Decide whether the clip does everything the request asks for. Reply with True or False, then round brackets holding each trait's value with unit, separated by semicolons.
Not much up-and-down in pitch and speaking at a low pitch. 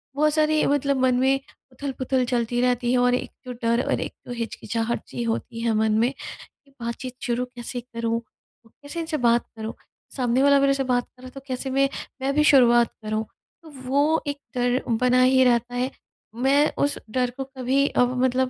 False (2.3 semitones; 250 Hz)